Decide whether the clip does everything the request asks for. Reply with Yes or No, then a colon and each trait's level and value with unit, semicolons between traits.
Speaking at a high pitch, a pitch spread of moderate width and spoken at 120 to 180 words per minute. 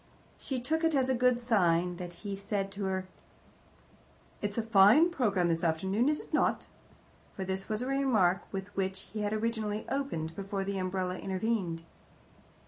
Yes: high, 200 Hz; average, 3.8 semitones; average, 170 wpm